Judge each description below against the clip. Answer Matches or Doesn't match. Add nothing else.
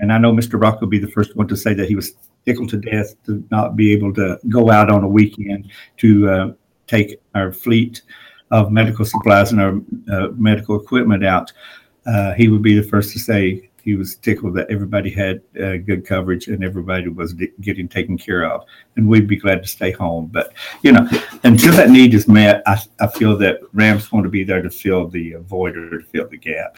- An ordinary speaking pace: Doesn't match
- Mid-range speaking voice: Doesn't match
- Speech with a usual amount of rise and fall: Doesn't match